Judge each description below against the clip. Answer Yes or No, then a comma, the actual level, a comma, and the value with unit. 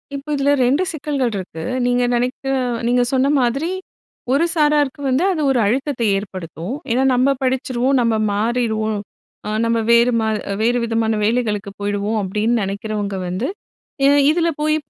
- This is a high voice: Yes, high, 245 Hz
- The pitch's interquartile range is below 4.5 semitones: Yes, average, 4.1 semitones